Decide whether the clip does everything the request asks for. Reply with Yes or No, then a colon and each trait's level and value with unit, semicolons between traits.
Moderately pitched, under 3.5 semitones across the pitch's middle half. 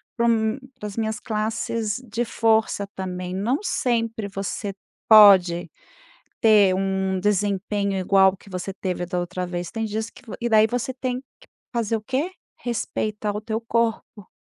No: high, 210 Hz; average, 3.0 semitones